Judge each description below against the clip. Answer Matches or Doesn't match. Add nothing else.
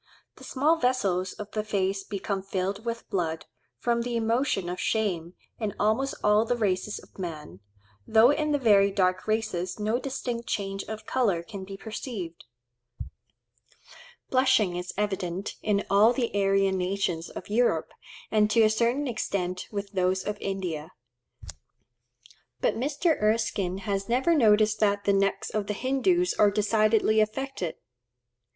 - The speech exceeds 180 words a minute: Doesn't match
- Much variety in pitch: Doesn't match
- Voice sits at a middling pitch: Doesn't match